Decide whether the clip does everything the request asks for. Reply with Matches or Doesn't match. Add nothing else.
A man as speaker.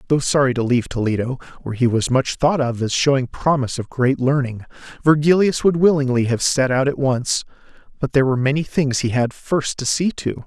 Matches